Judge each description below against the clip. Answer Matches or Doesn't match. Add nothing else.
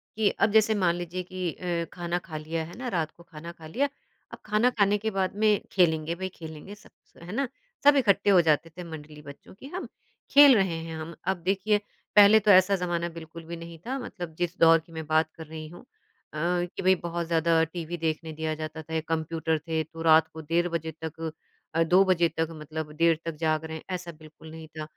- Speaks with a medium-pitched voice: Matches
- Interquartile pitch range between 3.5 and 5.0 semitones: Doesn't match